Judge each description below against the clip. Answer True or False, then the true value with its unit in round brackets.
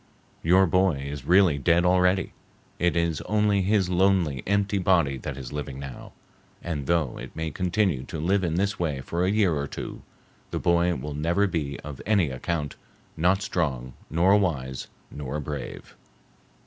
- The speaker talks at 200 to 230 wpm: False (165 wpm)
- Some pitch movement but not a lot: True (4.6 semitones)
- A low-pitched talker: True (85 Hz)